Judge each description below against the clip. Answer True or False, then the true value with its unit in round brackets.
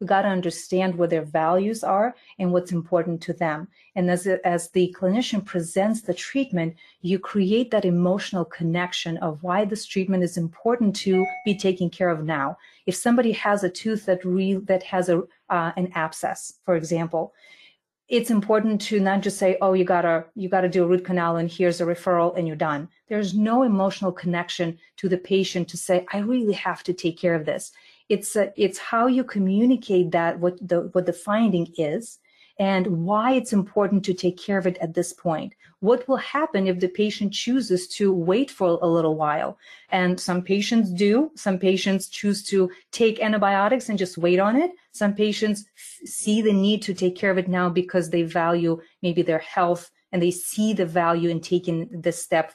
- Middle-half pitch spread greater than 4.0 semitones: False (2.9 semitones)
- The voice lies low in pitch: False (185 Hz)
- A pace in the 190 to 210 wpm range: True (200 wpm)